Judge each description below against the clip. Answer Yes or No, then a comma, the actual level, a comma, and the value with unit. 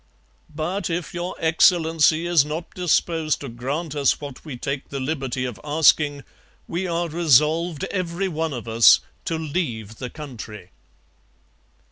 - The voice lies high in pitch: No, medium, 155 Hz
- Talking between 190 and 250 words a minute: No, average, 140 wpm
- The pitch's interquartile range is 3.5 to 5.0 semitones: Yes, average, 3.8 semitones